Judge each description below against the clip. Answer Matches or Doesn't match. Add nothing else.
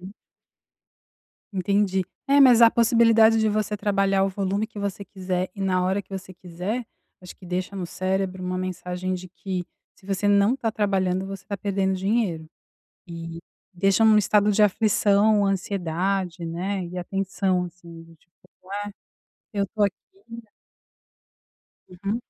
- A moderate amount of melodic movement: Doesn't match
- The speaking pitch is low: Doesn't match